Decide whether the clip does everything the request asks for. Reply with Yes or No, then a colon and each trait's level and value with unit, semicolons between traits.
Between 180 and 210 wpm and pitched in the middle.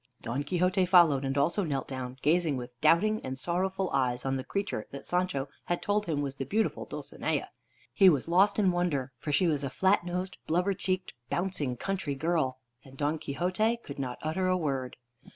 Yes: average, 190 wpm; medium, 160 Hz